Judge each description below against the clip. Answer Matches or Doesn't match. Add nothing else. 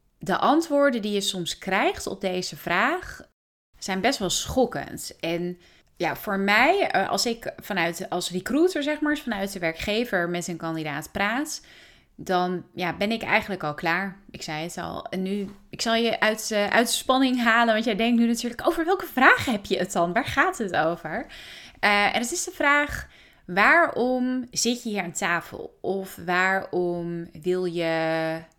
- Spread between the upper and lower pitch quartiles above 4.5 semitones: Matches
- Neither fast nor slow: Matches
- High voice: Matches